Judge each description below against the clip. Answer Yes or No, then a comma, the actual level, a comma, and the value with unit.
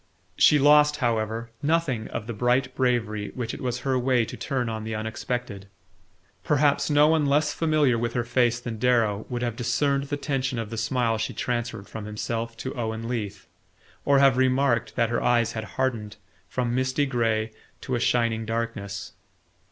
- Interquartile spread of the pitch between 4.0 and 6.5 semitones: No, average, 2.8 semitones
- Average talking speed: Yes, average, 175 wpm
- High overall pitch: No, low, 120 Hz